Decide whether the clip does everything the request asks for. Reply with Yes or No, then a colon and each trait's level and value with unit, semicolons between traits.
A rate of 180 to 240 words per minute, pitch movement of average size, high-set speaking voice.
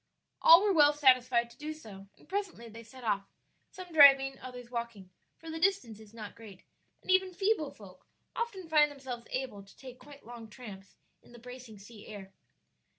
No: average, 185 wpm; wide, 5.7 semitones; very high, 250 Hz